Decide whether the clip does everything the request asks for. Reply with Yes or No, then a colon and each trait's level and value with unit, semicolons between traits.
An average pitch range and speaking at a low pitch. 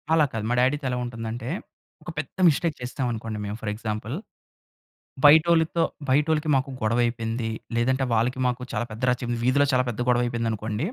Yes: average, 3.4 semitones; low, 125 Hz